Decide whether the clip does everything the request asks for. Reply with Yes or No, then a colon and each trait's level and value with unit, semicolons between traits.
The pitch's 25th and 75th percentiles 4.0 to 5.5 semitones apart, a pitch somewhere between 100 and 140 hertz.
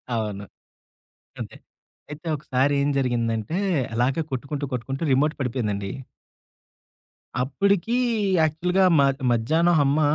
Yes: average, 4.4 semitones; low, 135 Hz